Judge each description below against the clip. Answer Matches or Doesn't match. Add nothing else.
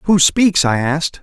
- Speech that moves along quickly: Doesn't match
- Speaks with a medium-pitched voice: Matches